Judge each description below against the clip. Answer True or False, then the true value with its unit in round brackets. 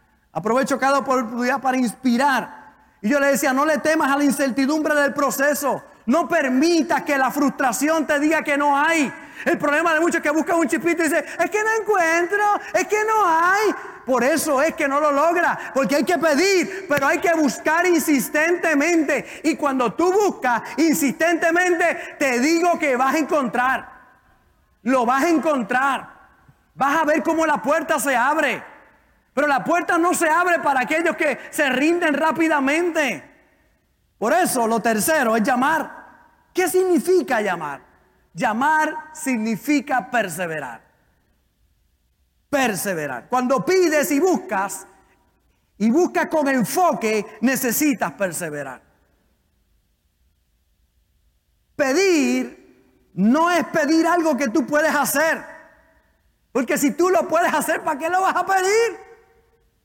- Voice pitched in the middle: False (300 Hz)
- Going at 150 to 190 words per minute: False (140 wpm)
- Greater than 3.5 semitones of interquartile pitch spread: True (3.9 semitones)